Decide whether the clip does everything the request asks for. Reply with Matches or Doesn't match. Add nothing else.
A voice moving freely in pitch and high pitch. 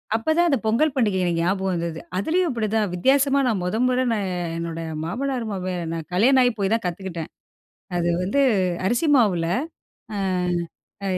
Matches